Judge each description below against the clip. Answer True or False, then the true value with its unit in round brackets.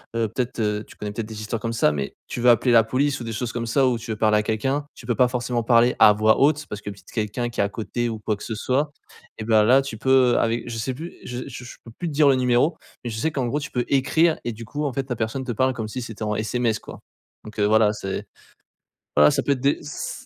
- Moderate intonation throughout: True (3.2 semitones)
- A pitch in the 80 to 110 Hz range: False (120 Hz)